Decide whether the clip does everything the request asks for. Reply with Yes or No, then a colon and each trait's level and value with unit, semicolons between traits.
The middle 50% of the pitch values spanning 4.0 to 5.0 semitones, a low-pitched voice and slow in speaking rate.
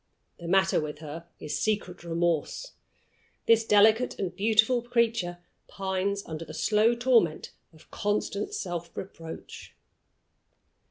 No: average, 4.5 semitones; high, 195 Hz; slow, 115 wpm